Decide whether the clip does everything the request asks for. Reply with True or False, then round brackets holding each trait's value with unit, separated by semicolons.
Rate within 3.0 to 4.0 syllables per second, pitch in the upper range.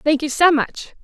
False (4.4 syllables/s; 300 Hz)